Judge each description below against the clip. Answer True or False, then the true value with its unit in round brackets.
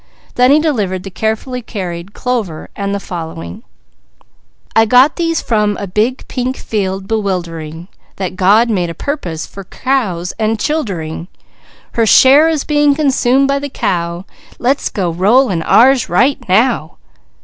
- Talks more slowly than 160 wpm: True (150 wpm)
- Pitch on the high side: True (215 Hz)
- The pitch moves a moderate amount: False (6.3 semitones)